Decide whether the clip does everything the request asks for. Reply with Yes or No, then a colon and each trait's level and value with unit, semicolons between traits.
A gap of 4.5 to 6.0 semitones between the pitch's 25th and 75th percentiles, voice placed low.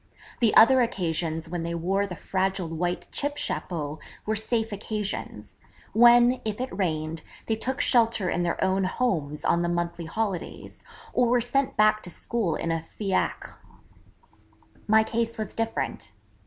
No: average, 5.1 semitones; high, 195 Hz